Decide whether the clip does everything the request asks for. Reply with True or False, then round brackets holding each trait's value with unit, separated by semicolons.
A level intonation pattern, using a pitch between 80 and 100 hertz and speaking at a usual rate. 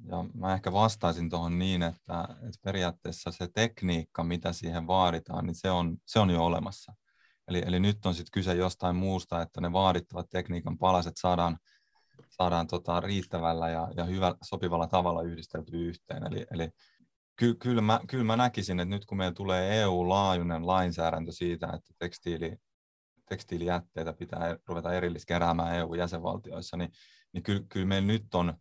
False (1.9 semitones; 90 Hz; 160 wpm)